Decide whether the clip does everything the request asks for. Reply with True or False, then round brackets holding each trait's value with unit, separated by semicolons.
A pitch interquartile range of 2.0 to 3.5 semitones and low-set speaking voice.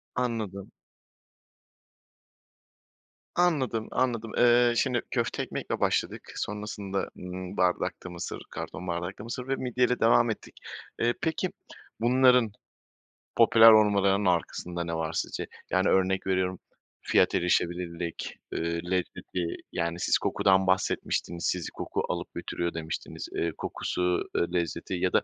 False (4.9 semitones; 95 Hz)